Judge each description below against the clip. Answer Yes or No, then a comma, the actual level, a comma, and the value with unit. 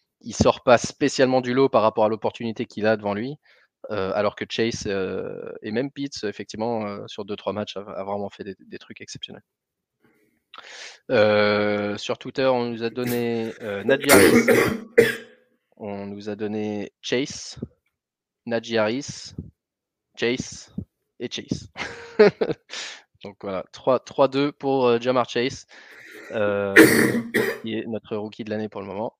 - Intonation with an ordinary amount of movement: Yes, average, 3.5 semitones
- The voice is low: Yes, low, 115 Hz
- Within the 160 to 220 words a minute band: No, average, 150 wpm